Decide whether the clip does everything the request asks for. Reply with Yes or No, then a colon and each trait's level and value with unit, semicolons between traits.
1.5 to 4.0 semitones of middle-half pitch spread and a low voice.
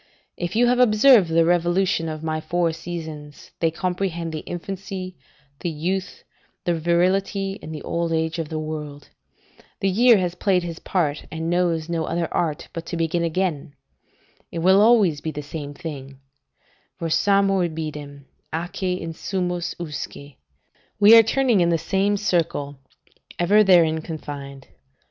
No: average, 3.1 semitones; medium, 170 Hz